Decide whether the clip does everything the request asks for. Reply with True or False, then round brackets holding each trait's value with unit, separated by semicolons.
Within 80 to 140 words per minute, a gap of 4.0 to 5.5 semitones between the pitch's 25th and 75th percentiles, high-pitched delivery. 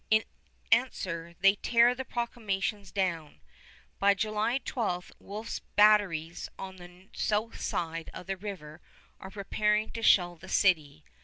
False (135 wpm; 3.4 semitones; 195 Hz)